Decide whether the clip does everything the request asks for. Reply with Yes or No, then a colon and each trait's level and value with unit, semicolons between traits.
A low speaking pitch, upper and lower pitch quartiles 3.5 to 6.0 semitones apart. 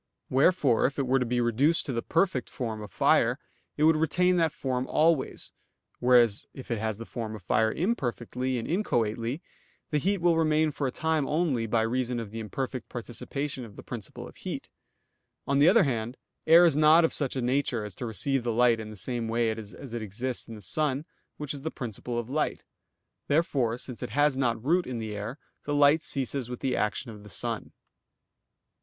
Yes: low, 125 Hz; average, 4.5 semitones